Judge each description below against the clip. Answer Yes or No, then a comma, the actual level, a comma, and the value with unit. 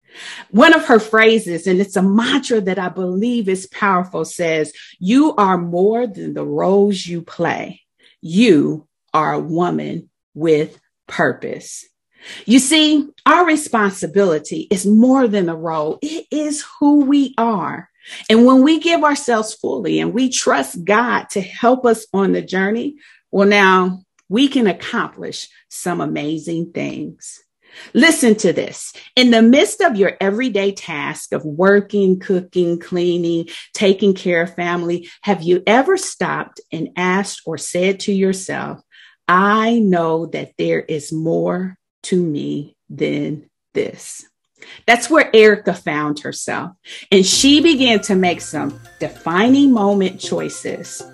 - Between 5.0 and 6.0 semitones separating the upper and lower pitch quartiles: Yes, average, 5.3 semitones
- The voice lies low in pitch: No, high, 195 Hz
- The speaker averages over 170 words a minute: No, average, 140 wpm